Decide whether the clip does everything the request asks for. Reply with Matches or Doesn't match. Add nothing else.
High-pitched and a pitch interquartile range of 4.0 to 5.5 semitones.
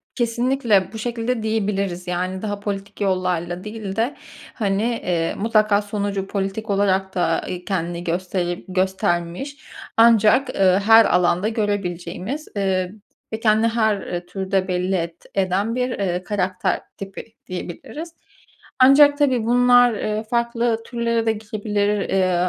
Doesn't match